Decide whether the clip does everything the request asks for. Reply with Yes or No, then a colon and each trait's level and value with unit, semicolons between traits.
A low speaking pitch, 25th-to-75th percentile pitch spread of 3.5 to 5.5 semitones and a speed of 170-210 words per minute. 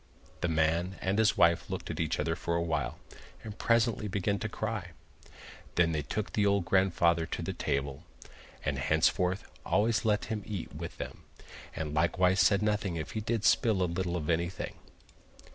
Yes: very low, 90 Hz; average, 4.1 semitones; average, 180 wpm